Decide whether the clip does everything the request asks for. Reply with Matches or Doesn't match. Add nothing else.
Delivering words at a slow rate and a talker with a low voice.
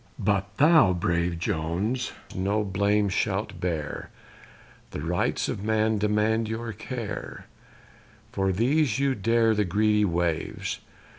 Matches